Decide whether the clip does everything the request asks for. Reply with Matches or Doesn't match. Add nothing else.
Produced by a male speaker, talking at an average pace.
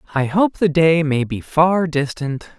Matches